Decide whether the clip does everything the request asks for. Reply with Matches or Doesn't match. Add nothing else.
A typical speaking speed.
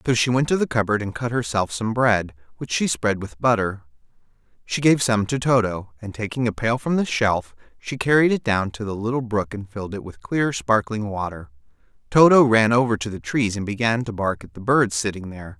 Doesn't match